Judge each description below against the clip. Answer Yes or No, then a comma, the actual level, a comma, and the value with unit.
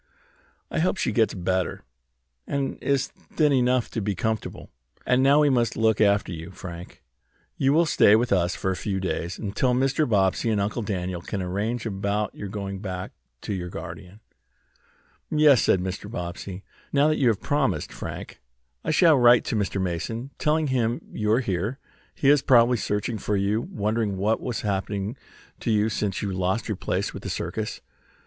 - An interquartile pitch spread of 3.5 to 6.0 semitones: Yes, average, 4.6 semitones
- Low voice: Yes, low, 105 Hz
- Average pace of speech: Yes, average, 180 wpm